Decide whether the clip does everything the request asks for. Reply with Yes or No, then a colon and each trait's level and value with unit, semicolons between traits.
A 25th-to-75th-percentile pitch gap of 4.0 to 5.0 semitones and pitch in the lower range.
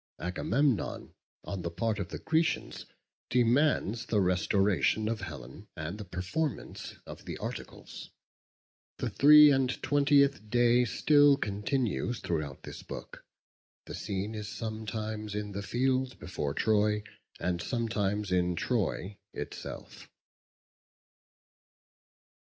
Yes: average, 4.5 semitones; low, 105 Hz